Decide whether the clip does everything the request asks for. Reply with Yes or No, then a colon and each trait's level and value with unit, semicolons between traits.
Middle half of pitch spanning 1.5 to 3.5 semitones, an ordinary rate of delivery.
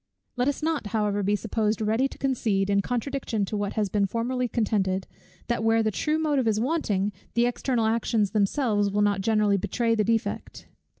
Yes: average, 3.0 semitones; average, 185 wpm